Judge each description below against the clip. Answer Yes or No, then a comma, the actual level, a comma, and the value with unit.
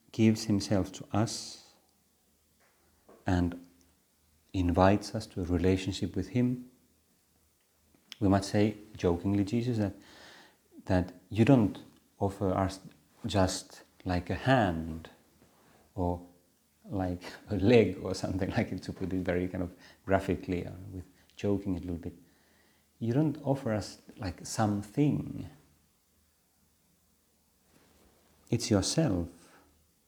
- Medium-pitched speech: No, very low, 95 Hz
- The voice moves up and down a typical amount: Yes, average, 3.1 semitones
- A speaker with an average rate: Yes, average, 110 wpm